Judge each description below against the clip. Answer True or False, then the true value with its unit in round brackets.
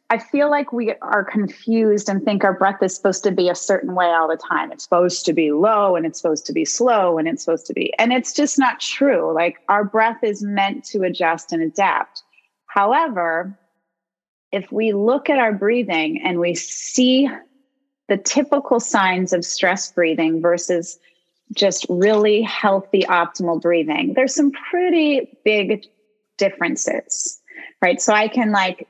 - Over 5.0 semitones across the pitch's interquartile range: True (5.4 semitones)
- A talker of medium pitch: False (200 Hz)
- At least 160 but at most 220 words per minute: True (170 wpm)